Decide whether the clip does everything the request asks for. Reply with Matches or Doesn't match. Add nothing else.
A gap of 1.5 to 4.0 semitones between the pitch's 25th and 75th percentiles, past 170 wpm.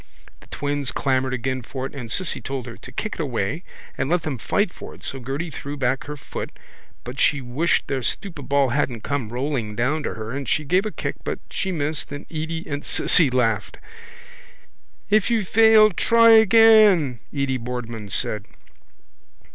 Doesn't match